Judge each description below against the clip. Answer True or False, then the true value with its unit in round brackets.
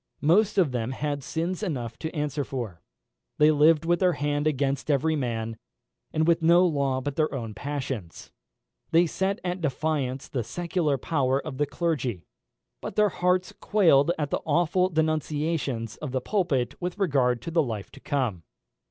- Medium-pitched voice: True (150 Hz)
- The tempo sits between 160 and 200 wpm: True (170 wpm)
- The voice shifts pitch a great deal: False (4.2 semitones)